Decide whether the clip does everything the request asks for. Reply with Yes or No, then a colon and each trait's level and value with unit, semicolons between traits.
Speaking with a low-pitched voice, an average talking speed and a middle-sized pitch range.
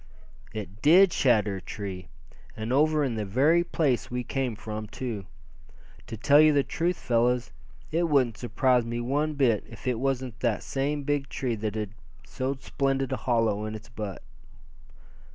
Yes: low, 125 Hz; average, 170 wpm; average, 4.3 semitones